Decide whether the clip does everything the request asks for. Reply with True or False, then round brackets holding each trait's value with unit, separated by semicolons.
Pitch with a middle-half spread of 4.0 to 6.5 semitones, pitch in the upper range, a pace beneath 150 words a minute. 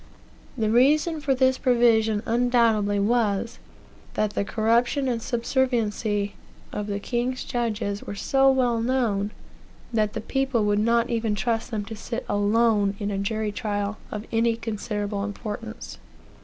False (2.7 semitones; 225 Hz; 140 wpm)